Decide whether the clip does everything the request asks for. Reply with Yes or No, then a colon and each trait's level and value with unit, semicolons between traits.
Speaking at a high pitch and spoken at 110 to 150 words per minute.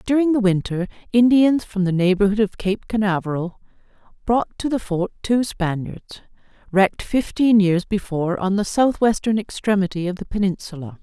Yes: high, 205 Hz; average, 145 wpm